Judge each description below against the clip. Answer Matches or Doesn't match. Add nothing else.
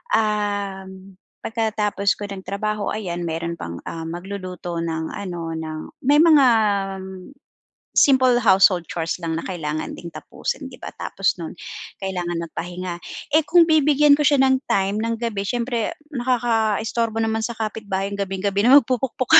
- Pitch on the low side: Doesn't match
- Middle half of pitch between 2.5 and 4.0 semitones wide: Doesn't match